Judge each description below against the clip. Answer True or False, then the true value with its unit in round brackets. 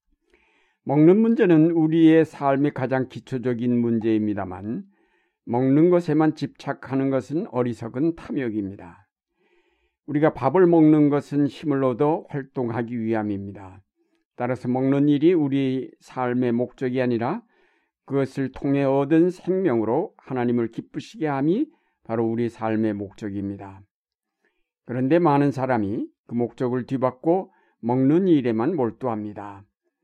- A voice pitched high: False (130 Hz)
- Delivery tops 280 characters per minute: False (275 characters per minute)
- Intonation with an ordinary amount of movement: True (4.8 semitones)